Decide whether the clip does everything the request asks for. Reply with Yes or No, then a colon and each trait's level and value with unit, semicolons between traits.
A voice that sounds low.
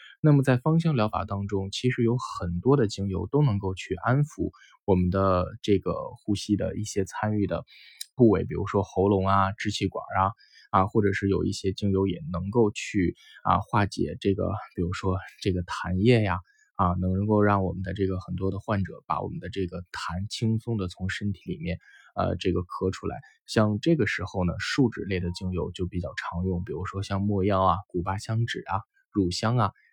Yes: low, 100 Hz